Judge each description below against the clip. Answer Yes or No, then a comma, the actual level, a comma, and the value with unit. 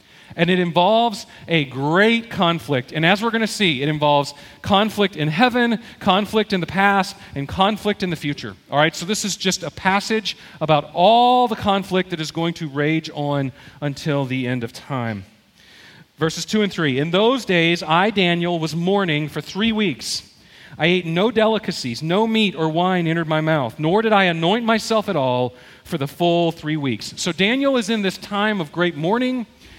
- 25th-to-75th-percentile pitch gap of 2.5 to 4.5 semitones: No, average, 5.3 semitones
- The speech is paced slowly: No, average, 190 wpm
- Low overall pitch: No, medium, 175 Hz